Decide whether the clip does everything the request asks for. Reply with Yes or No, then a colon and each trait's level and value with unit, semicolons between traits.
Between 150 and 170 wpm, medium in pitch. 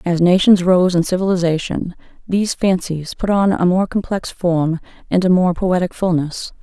Yes: average, 165 wpm; medium, 180 Hz